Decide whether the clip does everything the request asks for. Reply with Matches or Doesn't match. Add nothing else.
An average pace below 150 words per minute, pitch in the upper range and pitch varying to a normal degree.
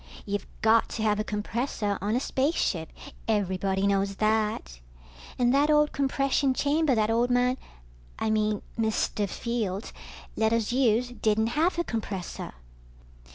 Matches